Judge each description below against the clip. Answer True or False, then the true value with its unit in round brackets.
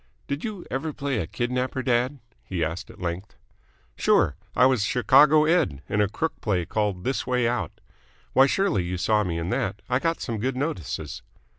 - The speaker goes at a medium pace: True (185 wpm)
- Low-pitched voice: True (120 Hz)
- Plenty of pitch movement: True (6.2 semitones)